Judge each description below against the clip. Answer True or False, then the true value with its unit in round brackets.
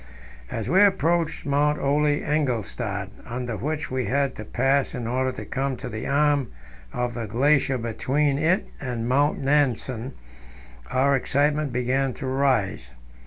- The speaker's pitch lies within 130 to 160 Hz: True (135 Hz)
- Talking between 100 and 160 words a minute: True (145 wpm)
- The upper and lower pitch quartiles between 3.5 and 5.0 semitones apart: False (3.1 semitones)